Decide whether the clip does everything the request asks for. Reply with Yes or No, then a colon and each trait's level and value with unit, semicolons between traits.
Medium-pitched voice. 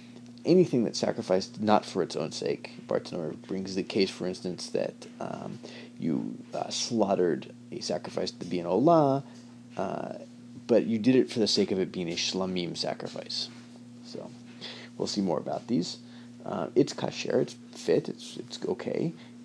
No: low, 120 Hz